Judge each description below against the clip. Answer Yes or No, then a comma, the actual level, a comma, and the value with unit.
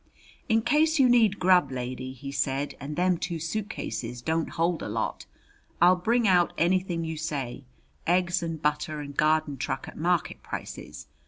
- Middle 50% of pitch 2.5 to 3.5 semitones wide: No, average, 4.3 semitones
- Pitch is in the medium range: Yes, medium, 165 Hz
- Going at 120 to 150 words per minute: No, average, 165 wpm